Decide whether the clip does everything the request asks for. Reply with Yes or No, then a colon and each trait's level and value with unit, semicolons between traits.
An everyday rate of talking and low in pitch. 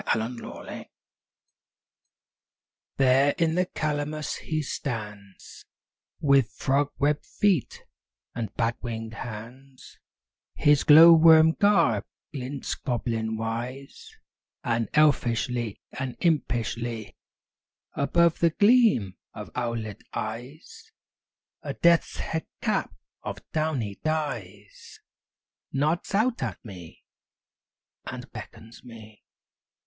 No: slow, 100 wpm; low, 130 Hz